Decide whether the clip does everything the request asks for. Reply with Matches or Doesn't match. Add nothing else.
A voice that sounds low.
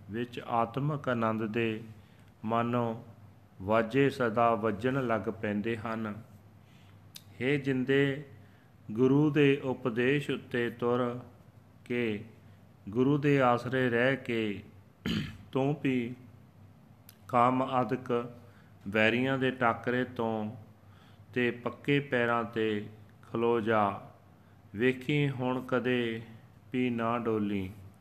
Matches